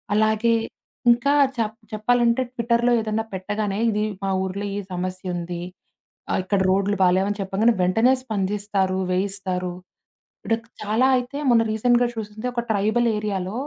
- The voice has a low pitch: No, high, 210 Hz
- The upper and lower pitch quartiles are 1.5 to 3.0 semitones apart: No, average, 3.5 semitones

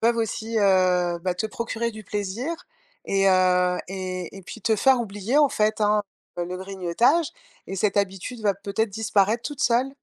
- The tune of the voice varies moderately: Yes, average, 3.5 semitones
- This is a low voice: No, high, 205 Hz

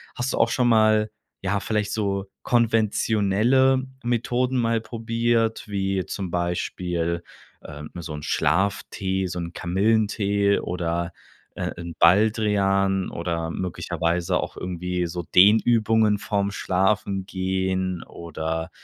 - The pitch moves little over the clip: No, average, 3.7 semitones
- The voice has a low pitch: Yes, low, 100 Hz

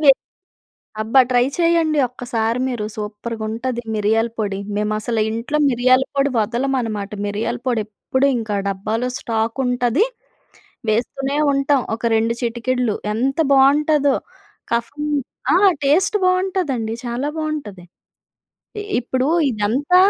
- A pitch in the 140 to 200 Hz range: No, high, 245 Hz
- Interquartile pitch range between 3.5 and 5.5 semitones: Yes, average, 3.8 semitones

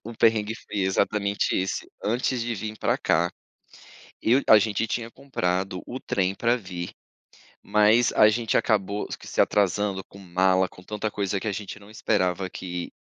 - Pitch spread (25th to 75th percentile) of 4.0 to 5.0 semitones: No, average, 2.7 semitones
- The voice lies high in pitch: No, low, 105 Hz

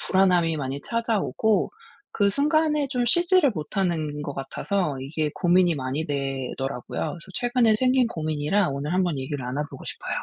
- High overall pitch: No, medium, 175 Hz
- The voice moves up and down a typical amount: No, wide, 7.8 semitones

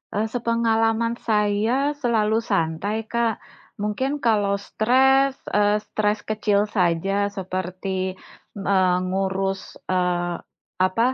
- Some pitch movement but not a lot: Yes, average, 3.1 semitones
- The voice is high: Yes, high, 210 Hz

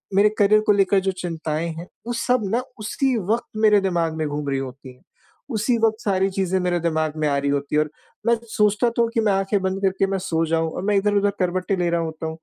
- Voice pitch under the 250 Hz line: Yes, high, 190 Hz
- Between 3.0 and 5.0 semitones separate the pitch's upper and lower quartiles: Yes, average, 4.4 semitones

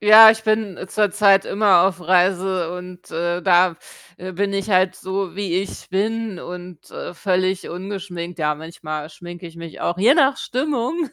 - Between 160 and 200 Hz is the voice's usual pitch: Yes, medium, 185 Hz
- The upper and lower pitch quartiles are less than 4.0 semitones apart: Yes, average, 2.9 semitones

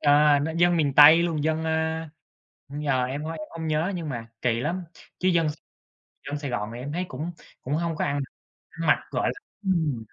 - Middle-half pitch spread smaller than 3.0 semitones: Yes, narrow, 2.5 semitones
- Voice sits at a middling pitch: Yes, medium, 155 Hz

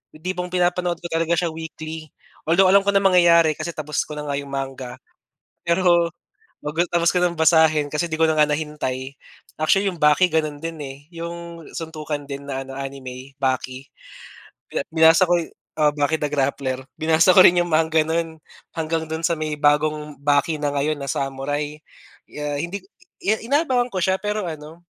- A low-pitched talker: No, medium, 160 Hz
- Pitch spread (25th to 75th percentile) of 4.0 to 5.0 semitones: No, average, 2.8 semitones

